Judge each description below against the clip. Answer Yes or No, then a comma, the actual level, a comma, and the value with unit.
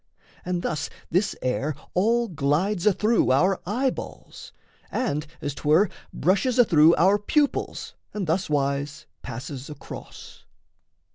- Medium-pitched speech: Yes, medium, 175 Hz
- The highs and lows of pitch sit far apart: Yes, wide, 6.1 semitones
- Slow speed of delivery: Yes, slow, 110 wpm